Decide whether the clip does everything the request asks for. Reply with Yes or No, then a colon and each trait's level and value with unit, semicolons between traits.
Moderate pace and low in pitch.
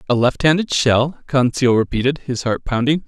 Yes: average, 155 wpm; low, 130 Hz